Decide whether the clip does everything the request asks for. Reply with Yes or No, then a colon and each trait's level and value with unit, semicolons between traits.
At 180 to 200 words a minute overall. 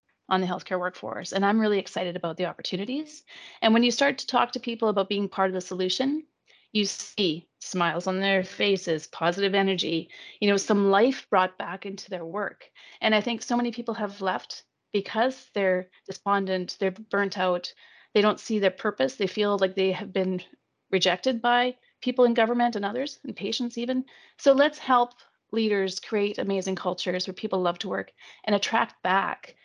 Yes: average, 185 wpm